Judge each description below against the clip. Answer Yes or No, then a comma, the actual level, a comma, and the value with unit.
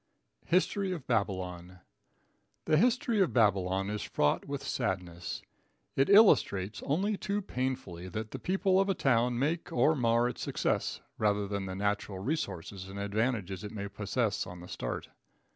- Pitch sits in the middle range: No, low, 110 Hz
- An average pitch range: No, wide, 7.4 semitones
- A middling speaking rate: Yes, average, 155 wpm